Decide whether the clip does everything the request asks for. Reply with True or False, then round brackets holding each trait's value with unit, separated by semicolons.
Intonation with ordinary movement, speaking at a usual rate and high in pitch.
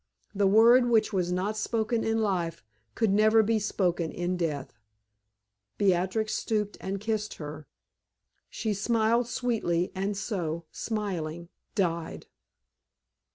False (4.0 semitones; 115 wpm; 200 Hz)